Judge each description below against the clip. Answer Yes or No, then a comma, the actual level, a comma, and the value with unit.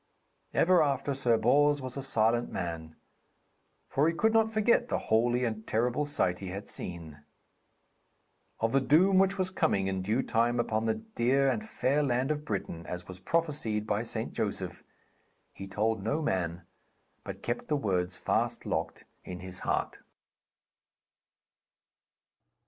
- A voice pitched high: No, low, 120 Hz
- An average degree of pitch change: No, wide, 7.1 semitones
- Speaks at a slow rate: No, average, 150 wpm